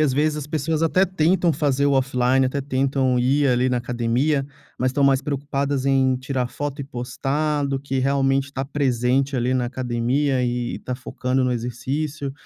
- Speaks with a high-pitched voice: No, low, 135 Hz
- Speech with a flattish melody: Yes, narrow, 2.0 semitones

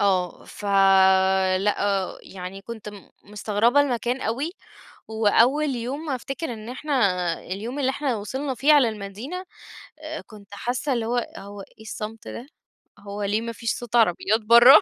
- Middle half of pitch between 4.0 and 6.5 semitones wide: Yes, average, 4.3 semitones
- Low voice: No, high, 225 Hz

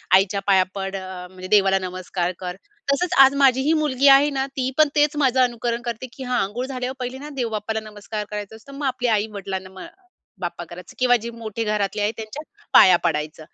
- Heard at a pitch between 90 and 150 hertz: No, high, 220 Hz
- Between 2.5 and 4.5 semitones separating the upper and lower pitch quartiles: No, average, 5.3 semitones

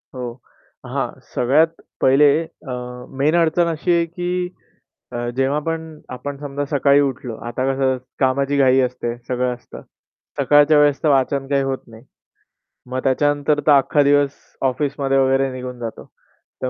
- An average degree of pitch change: No, narrow, 2.3 semitones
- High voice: No, medium, 140 Hz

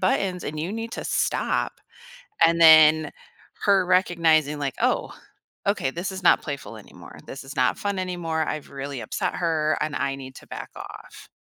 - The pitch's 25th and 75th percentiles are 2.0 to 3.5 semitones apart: No, average, 4.1 semitones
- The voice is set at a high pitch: No, medium, 160 Hz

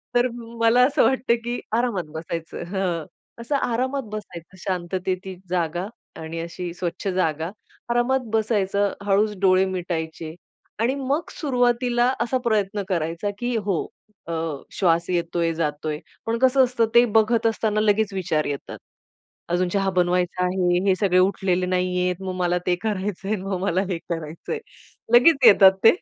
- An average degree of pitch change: Yes, average, 4.5 semitones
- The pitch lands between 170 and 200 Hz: Yes, high, 190 Hz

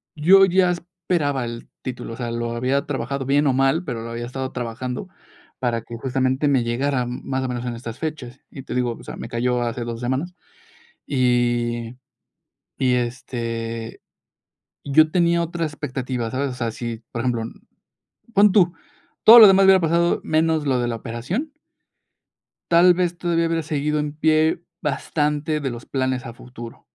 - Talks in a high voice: No, low, 130 Hz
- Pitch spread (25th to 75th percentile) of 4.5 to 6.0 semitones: Yes, average, 4.8 semitones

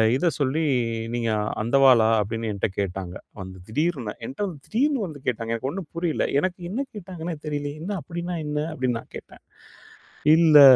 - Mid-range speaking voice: Yes, medium, 145 Hz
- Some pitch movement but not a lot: No, wide, 6.9 semitones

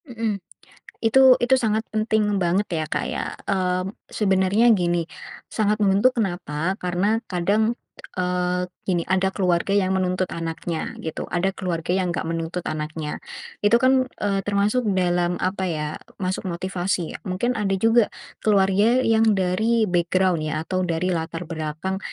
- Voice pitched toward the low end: No, medium, 185 Hz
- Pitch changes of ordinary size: Yes, average, 3.2 semitones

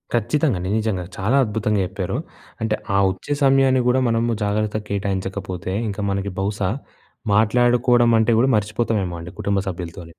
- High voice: No, low, 105 Hz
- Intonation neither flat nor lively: Yes, average, 3.4 semitones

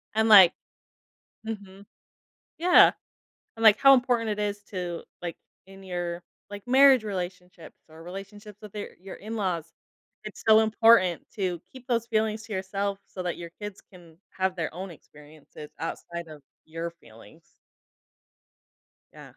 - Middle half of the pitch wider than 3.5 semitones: Yes, average, 4.0 semitones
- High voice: Yes, high, 195 Hz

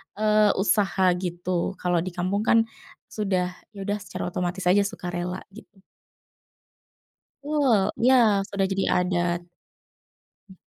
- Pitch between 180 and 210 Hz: Yes, high, 190 Hz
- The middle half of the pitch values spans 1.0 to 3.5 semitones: Yes, narrow, 2.5 semitones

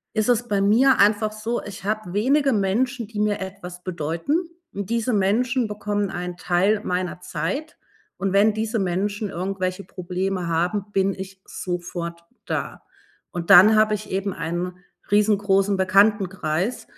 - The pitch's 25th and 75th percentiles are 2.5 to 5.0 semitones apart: Yes, average, 2.9 semitones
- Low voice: No, high, 200 Hz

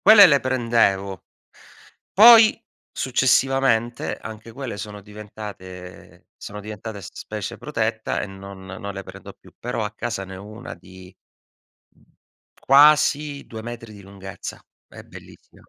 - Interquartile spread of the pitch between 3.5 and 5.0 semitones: Yes, average, 4.7 semitones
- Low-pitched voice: Yes, low, 110 Hz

